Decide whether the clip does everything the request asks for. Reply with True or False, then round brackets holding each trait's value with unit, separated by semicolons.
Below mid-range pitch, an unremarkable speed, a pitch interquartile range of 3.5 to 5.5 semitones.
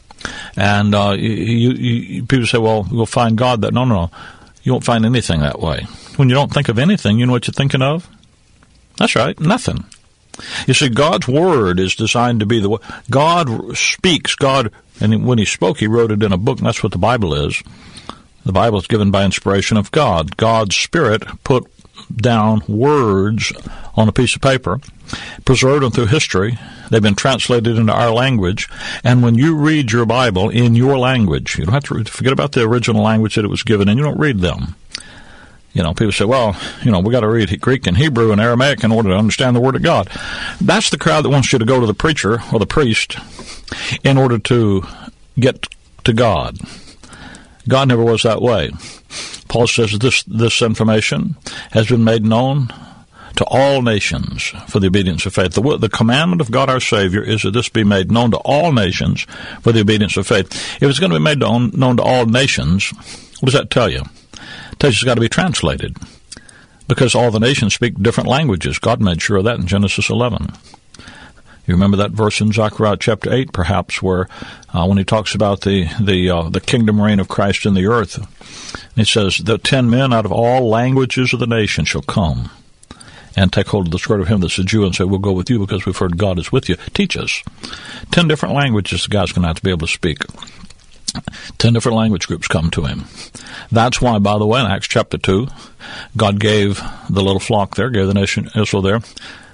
False (110 Hz; 210 wpm; 3.8 semitones)